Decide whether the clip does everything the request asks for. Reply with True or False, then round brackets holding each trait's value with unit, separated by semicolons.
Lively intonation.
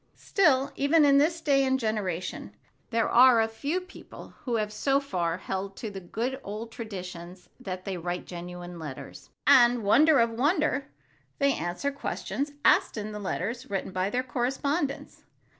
True (6.6 semitones)